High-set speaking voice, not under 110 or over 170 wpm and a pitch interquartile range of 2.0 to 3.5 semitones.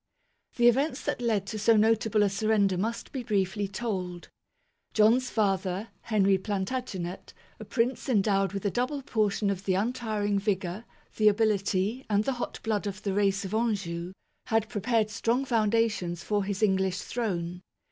Yes: high, 210 Hz; average, 160 wpm; average, 2.8 semitones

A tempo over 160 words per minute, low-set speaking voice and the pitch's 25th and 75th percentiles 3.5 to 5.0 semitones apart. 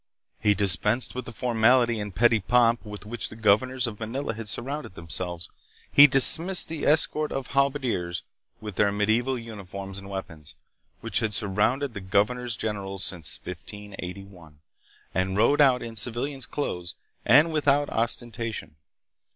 No: average, 145 wpm; low, 110 Hz; average, 4.6 semitones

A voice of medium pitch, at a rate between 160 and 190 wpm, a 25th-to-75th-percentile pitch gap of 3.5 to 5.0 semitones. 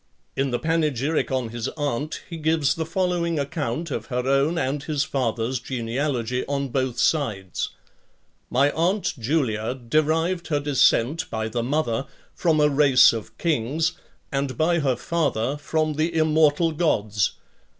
No: medium, 145 Hz; average, 145 wpm; average, 4.2 semitones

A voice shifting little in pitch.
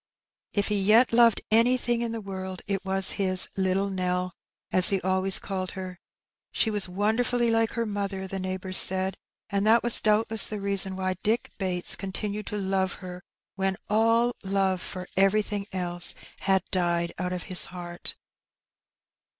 Yes: narrow, 2.3 semitones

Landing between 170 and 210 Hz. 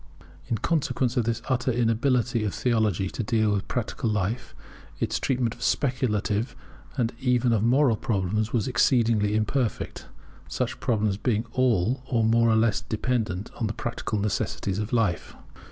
No: low, 115 Hz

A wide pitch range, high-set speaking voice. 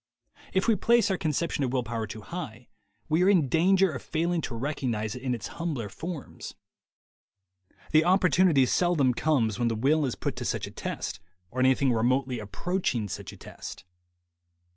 No: wide, 6.3 semitones; low, 135 Hz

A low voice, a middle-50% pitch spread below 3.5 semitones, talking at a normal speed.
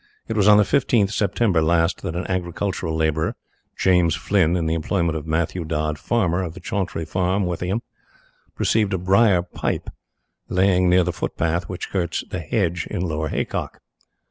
Yes: very low, 90 Hz; average, 2.9 semitones; average, 170 wpm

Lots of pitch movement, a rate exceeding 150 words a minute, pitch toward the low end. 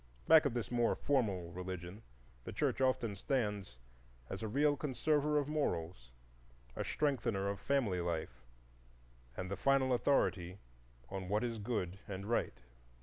No: wide, 6.6 semitones; average, 145 wpm; low, 110 Hz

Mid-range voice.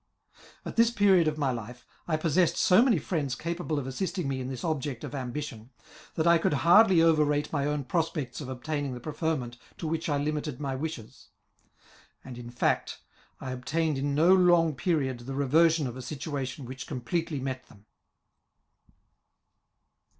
Yes: medium, 145 Hz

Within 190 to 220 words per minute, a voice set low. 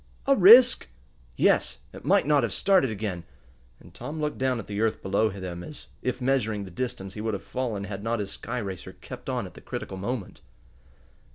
Yes: average, 200 wpm; low, 110 Hz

